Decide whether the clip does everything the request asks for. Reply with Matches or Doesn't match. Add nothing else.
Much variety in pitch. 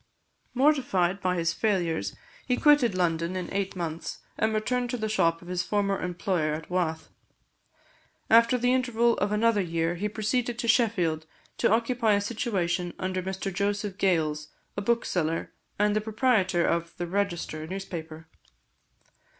Doesn't match